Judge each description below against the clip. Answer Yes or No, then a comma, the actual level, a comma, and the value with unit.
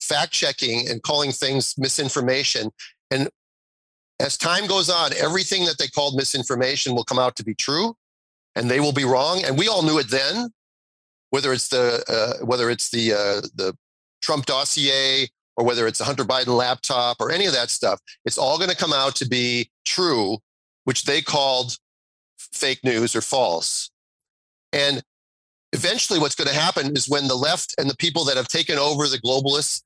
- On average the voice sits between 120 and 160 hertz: Yes, low, 135 Hz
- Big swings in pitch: No, average, 3.4 semitones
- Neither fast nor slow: Yes, average, 180 wpm